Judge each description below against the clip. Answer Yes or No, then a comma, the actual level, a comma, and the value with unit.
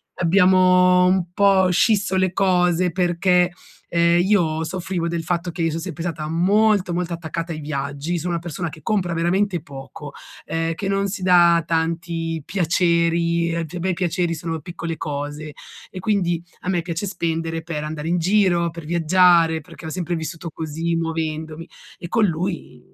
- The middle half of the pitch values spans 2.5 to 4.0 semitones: No, narrow, 1.9 semitones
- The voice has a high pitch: No, medium, 170 Hz